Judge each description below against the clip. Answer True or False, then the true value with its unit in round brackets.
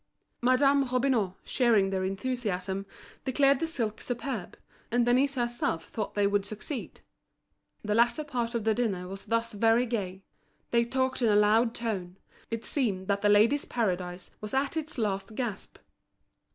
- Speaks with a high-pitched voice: True (230 Hz)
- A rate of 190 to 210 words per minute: False (155 wpm)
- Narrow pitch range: False (3.9 semitones)